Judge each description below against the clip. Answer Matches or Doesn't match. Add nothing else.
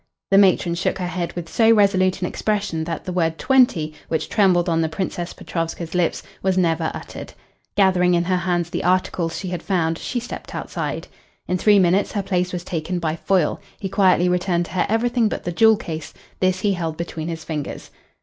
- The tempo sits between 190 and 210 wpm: Matches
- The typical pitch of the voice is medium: Matches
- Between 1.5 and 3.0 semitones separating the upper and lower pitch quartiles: Matches